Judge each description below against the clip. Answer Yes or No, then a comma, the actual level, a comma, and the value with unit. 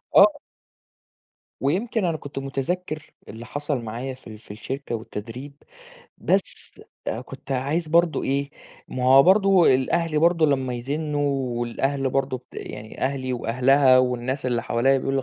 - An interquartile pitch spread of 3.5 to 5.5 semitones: No, average, 2.9 semitones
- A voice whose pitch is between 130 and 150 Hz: Yes, low, 135 Hz